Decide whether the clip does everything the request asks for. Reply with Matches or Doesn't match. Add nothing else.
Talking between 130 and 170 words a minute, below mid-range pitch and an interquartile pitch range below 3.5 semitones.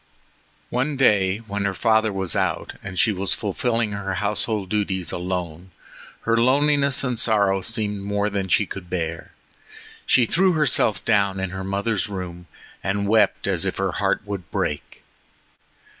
Matches